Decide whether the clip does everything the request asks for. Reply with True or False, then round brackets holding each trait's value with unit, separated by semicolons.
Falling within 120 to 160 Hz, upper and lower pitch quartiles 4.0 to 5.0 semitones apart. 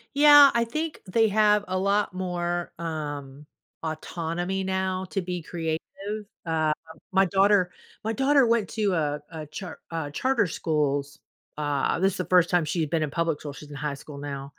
False (175 Hz; 4.5 semitones)